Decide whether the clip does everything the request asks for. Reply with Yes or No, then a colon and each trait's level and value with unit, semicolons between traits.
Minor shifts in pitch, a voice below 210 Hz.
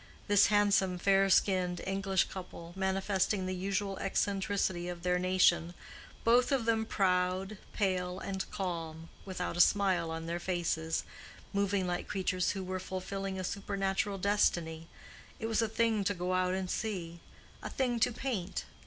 Yes: narrow, 1.9 semitones; high, 190 Hz